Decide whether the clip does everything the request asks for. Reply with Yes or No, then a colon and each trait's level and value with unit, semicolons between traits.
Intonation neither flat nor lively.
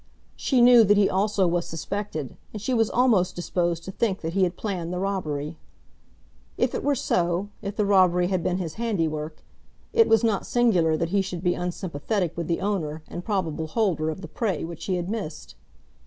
Yes: average, 3.6 semitones